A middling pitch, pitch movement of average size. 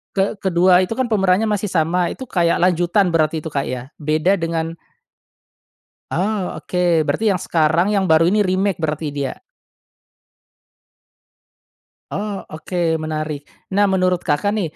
Yes: medium, 175 Hz; average, 3.4 semitones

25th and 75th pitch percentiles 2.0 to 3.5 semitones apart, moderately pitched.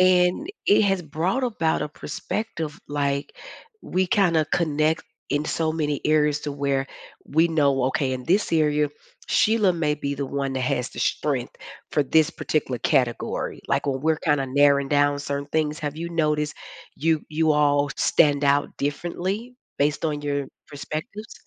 Yes: narrow, 2.5 semitones; medium, 150 Hz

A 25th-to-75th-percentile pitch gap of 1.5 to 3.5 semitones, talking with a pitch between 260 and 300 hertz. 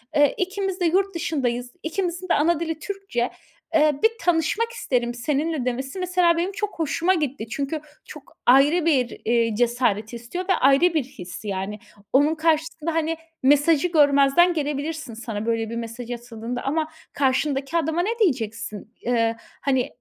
No: wide, 5.6 semitones; very high, 290 Hz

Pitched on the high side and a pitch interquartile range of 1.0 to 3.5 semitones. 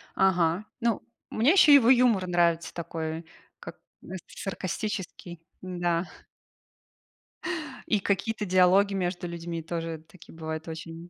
No: medium, 175 Hz; average, 3.1 semitones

